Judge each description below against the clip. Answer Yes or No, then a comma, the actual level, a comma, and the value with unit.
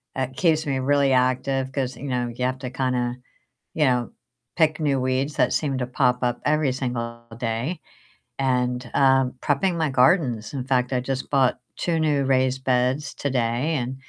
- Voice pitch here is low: Yes, low, 130 Hz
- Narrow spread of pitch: Yes, narrow, 2.0 semitones